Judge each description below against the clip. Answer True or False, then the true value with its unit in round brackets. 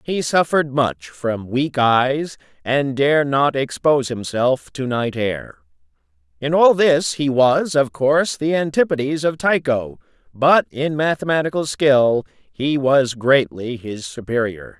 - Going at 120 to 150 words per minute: True (140 wpm)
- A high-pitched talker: False (135 Hz)